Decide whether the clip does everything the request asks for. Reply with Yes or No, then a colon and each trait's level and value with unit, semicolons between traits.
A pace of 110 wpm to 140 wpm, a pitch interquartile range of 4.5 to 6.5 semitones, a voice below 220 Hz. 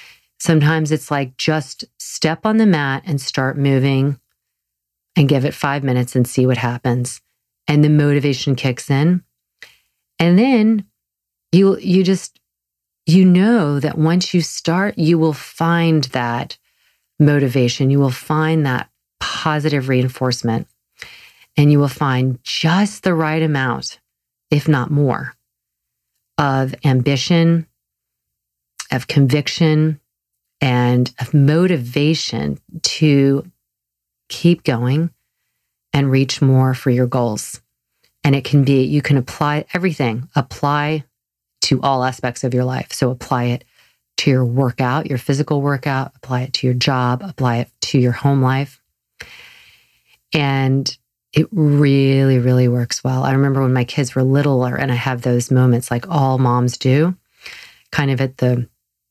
No: slow, 135 wpm; average, 3.3 semitones; low, 135 Hz